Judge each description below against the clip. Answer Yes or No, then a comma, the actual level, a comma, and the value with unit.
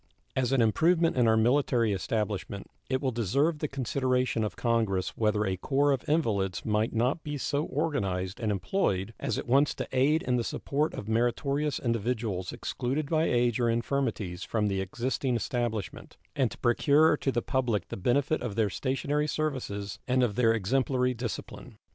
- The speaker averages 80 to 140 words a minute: No, average, 170 wpm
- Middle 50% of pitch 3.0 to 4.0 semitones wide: No, average, 4.4 semitones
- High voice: No, low, 120 Hz